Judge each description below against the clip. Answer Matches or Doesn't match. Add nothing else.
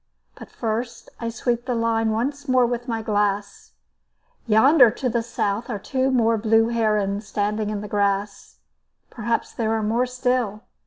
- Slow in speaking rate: Doesn't match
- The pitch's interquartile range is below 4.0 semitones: Matches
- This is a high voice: Matches